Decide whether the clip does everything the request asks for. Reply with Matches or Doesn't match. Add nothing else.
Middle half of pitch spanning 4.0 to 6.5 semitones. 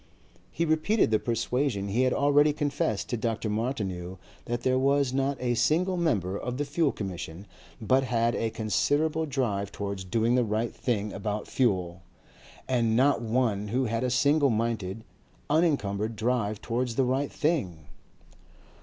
Matches